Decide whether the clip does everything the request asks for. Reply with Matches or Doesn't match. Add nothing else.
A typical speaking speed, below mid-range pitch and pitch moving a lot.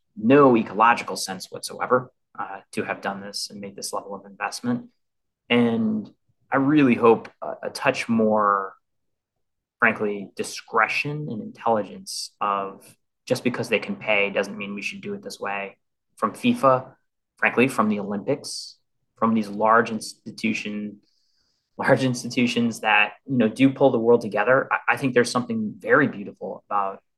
Matches